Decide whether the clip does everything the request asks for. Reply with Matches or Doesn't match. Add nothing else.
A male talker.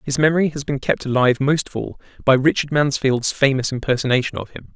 Matches